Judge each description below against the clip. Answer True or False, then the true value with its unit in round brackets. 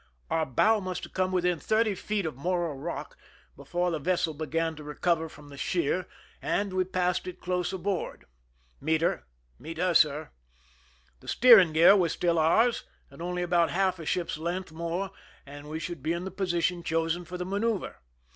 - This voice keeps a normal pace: True (185 wpm)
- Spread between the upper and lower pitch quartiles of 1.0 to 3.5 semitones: True (2.4 semitones)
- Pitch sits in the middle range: True (175 Hz)